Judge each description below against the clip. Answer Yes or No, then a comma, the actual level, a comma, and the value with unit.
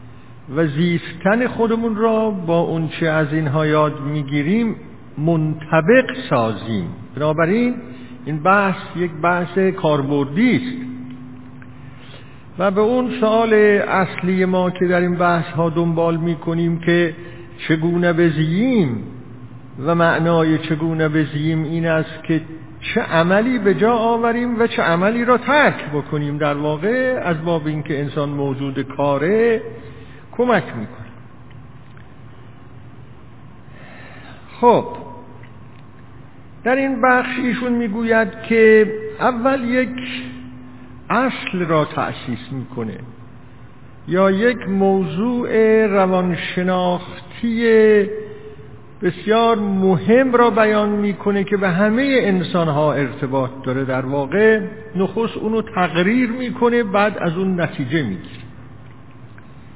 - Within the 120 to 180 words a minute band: No, slow, 105 wpm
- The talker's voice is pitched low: No, medium, 170 Hz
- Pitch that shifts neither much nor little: No, wide, 7.9 semitones